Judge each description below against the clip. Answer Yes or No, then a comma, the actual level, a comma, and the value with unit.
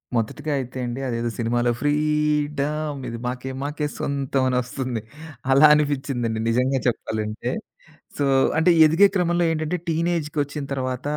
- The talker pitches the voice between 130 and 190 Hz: Yes, medium, 140 Hz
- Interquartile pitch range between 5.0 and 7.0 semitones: No, average, 3.5 semitones